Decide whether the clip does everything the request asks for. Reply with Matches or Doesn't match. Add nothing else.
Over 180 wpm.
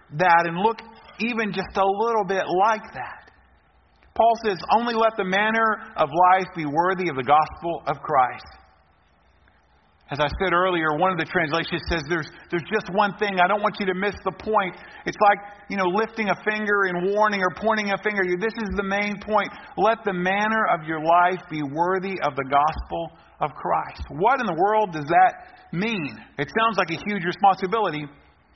Matches